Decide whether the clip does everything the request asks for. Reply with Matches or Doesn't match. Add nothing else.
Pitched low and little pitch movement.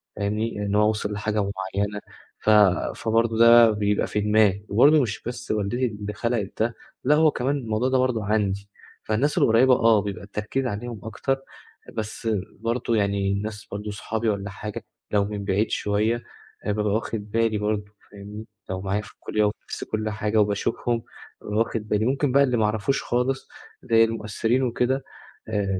Matches